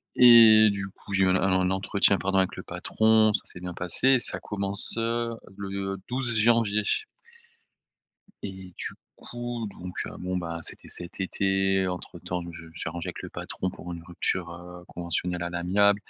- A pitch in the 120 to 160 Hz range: No, very low, 95 Hz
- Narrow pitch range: No, average, 3.4 semitones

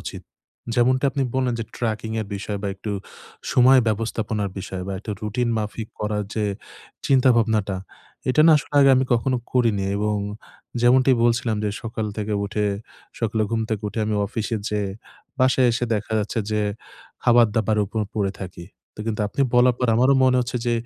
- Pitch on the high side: No, low, 110 Hz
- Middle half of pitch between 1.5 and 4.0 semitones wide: Yes, average, 2.7 semitones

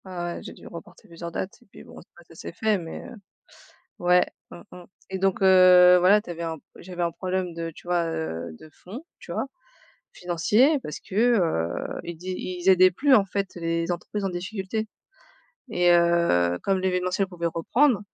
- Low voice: No, medium, 180 Hz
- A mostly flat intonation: Yes, narrow, 2.1 semitones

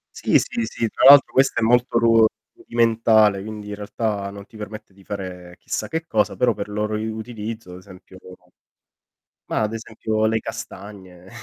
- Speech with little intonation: Yes, narrow, 2.1 semitones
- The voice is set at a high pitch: No, low, 110 Hz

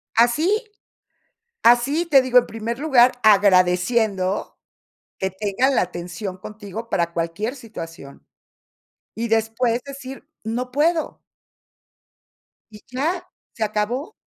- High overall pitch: Yes, high, 230 Hz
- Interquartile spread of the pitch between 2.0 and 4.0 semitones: No, average, 4.7 semitones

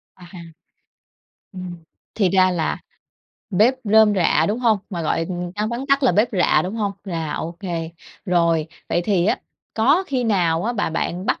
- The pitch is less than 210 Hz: Yes, high, 190 Hz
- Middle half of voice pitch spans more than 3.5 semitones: Yes, average, 4.0 semitones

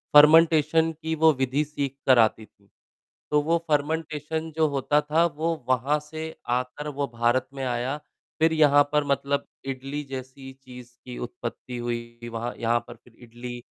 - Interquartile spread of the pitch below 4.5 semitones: Yes, average, 3.7 semitones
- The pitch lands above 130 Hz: Yes, medium, 140 Hz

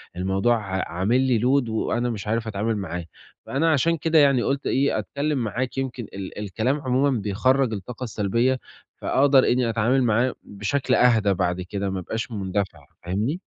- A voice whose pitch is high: No, low, 115 Hz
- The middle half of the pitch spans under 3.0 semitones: No, average, 4.7 semitones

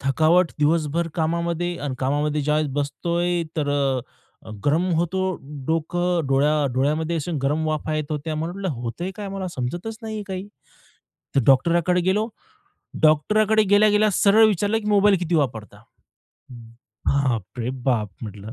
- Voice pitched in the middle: Yes, medium, 160 Hz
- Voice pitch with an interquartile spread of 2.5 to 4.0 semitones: No, average, 4.4 semitones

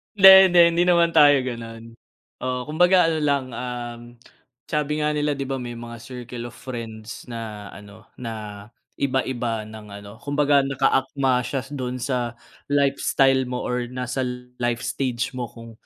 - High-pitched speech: No, low, 125 Hz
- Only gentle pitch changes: No, average, 3.2 semitones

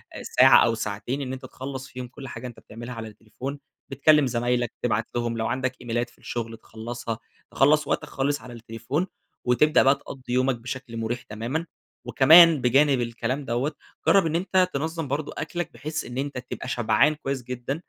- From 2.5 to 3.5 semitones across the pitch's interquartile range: Yes, average, 3.2 semitones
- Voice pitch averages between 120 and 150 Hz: Yes, low, 125 Hz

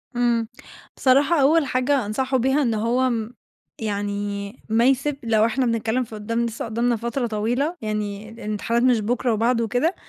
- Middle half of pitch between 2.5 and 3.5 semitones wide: Yes, average, 3.0 semitones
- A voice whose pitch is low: No, high, 235 Hz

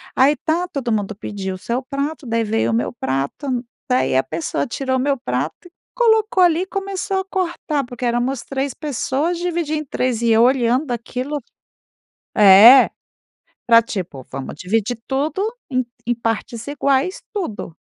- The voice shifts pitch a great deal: No, average, 5.0 semitones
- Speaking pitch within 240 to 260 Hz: Yes, very high, 255 Hz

